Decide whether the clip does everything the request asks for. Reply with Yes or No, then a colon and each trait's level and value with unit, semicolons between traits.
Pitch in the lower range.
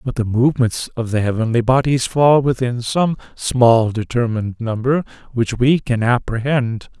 Yes: low, 120 Hz